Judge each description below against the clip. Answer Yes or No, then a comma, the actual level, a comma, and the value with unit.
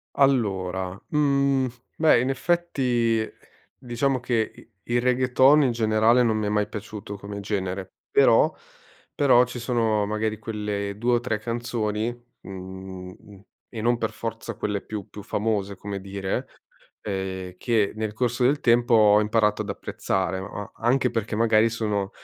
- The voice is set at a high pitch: No, low, 110 Hz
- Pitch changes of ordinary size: Yes, average, 3.1 semitones